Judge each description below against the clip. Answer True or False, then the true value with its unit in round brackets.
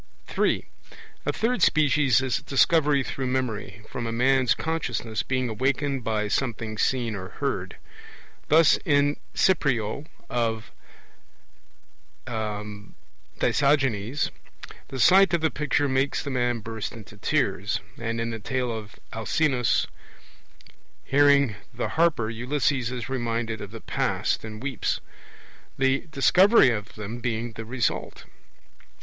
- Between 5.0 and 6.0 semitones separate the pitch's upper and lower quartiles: False (3.9 semitones)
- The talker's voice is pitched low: True (125 Hz)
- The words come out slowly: True (125 wpm)